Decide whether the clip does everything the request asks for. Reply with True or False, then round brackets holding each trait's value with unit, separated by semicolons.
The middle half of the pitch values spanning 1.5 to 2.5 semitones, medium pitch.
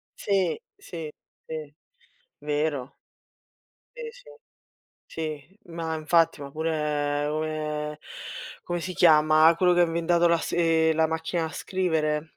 True (2.0 semitones; 160 Hz)